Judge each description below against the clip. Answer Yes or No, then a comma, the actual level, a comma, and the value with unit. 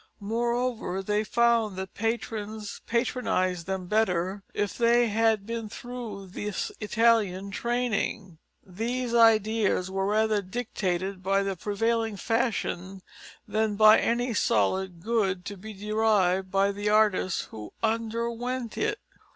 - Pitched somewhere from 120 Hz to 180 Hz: No, high, 215 Hz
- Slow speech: Yes, slow, 120 wpm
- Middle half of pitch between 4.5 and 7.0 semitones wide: No, average, 3.2 semitones